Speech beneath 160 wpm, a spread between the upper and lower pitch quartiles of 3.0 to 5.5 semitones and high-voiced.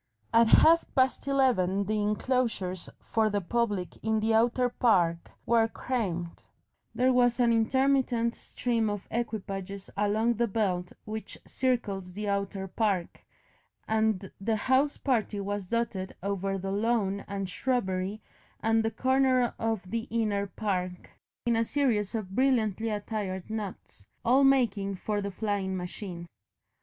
Yes: slow, 135 wpm; average, 3.3 semitones; high, 215 Hz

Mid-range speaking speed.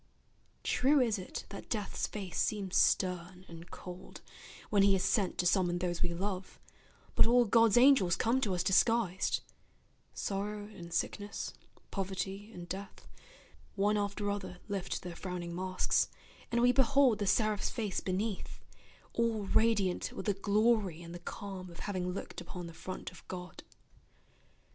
Yes: average, 155 wpm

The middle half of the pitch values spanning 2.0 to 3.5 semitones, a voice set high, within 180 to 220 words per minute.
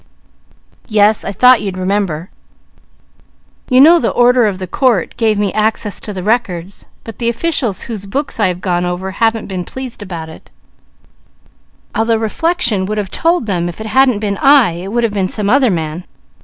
No: average, 4.3 semitones; high, 210 Hz; average, 185 wpm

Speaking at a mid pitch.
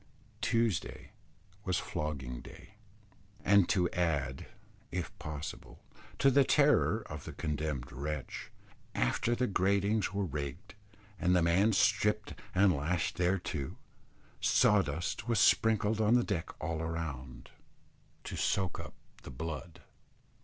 No: very low, 90 Hz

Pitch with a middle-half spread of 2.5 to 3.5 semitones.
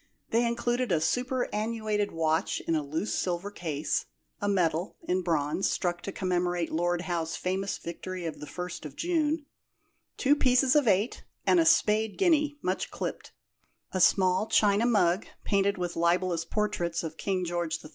No: average, 4.3 semitones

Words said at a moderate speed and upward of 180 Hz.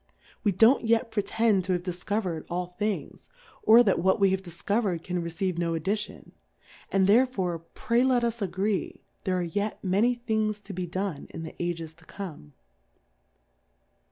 Yes: average, 160 wpm; high, 190 Hz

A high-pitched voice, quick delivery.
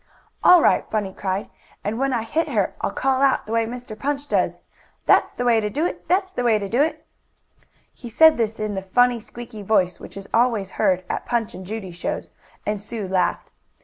Yes: high, 225 Hz; fast, 215 wpm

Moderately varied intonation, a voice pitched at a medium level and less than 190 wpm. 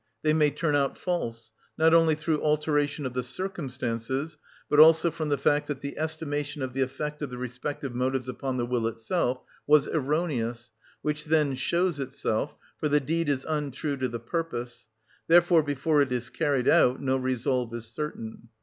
Yes: average, 3.4 semitones; medium, 145 Hz; average, 175 wpm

